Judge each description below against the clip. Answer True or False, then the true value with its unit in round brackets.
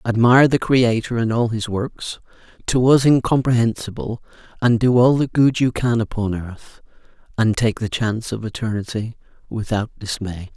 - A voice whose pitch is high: False (115 Hz)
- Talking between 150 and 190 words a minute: True (155 wpm)